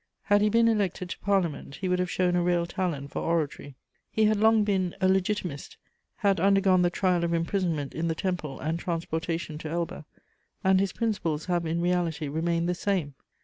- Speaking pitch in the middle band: Yes, medium, 175 Hz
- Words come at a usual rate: Yes, average, 190 wpm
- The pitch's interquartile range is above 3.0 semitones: No, average, 2.7 semitones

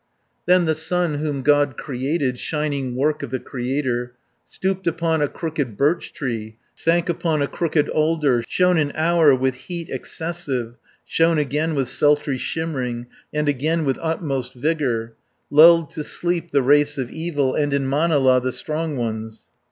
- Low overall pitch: No, medium, 145 Hz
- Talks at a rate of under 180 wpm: Yes, average, 160 wpm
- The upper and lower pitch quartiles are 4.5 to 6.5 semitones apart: No, average, 3.9 semitones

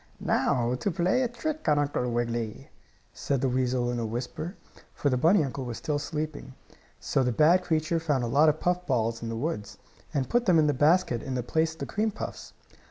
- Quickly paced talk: Yes, fast, 215 wpm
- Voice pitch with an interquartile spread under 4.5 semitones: No, average, 5.1 semitones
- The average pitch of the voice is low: No, medium, 145 Hz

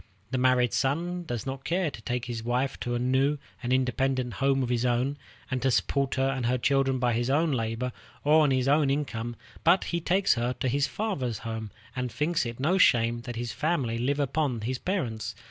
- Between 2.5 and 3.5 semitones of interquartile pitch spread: Yes, average, 3.0 semitones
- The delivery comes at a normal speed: No, fast, 215 wpm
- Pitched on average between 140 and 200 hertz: No, low, 130 Hz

